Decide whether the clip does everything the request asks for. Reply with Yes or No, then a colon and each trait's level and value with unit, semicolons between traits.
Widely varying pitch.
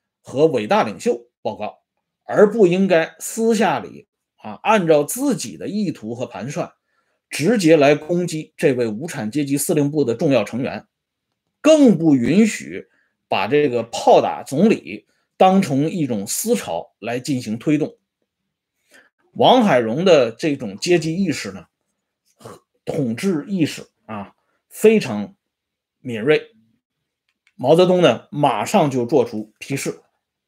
Yes: wide, 8.0 semitones